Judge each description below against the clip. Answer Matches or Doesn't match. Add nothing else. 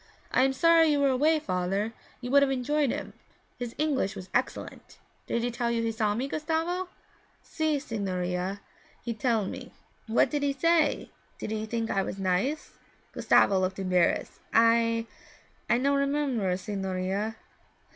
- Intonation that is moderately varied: Doesn't match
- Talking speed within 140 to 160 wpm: Matches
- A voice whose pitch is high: Matches